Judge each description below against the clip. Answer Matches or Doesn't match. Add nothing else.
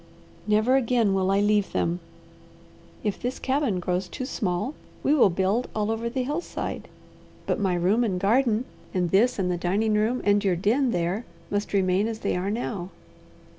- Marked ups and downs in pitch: Doesn't match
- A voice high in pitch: Matches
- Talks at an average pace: Matches